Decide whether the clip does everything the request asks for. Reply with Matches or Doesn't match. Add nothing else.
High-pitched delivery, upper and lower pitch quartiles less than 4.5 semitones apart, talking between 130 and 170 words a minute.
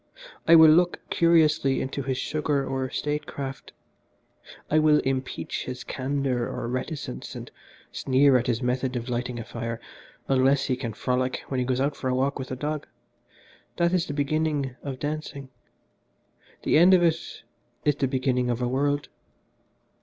Doesn't match